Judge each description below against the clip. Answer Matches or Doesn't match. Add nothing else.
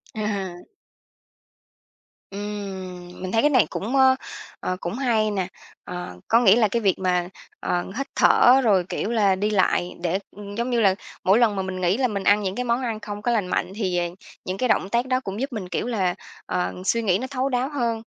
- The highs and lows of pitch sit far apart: Doesn't match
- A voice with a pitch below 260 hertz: Matches